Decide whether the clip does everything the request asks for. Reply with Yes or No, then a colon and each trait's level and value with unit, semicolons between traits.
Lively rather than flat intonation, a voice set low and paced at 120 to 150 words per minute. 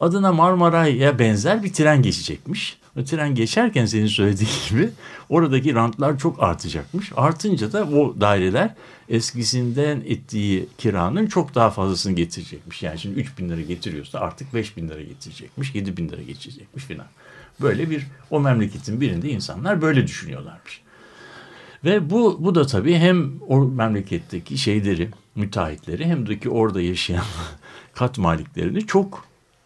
Yes: wide, 8.1 semitones; low, 130 Hz; fast, 140 wpm